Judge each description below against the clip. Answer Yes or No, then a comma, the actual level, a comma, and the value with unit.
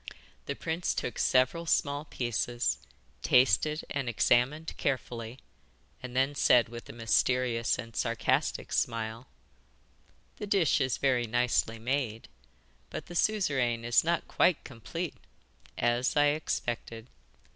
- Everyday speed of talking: No, slow, 120 wpm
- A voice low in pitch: Yes, low, 125 Hz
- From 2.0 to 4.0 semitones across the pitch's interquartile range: Yes, average, 3.7 semitones